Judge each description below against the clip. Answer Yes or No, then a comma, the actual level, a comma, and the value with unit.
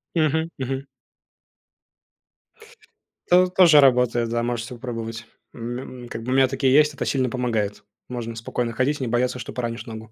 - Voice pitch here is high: No, low, 125 Hz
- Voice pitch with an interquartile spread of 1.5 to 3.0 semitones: Yes, narrow, 2.6 semitones